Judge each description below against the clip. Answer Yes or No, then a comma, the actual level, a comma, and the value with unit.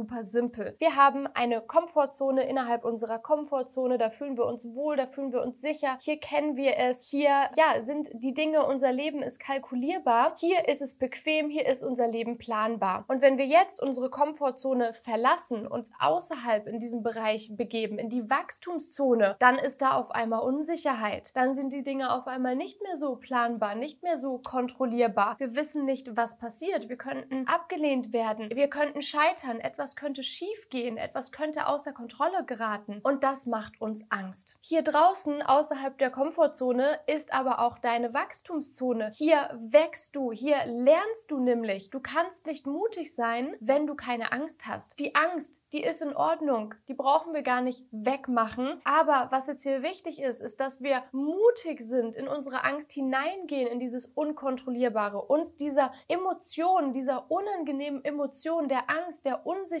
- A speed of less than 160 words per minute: No, average, 170 wpm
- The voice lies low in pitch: No, very high, 270 Hz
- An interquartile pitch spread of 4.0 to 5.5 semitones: No, average, 3.5 semitones